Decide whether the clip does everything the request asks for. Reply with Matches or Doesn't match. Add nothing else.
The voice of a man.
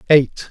Matches